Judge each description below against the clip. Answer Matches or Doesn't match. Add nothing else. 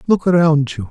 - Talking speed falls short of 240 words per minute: Matches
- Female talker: Doesn't match